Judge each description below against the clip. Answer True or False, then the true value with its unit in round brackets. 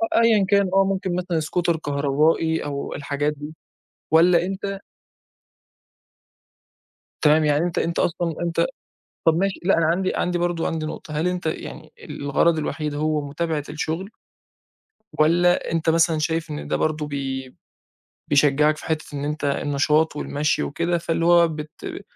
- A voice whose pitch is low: False (160 Hz)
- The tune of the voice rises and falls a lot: False (2.6 semitones)